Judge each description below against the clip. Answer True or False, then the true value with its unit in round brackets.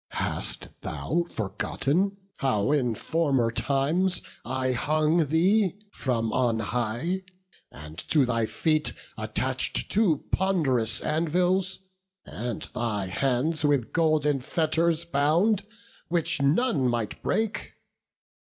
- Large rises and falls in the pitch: True (5.7 semitones)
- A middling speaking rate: False (105 wpm)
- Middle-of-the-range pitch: True (150 Hz)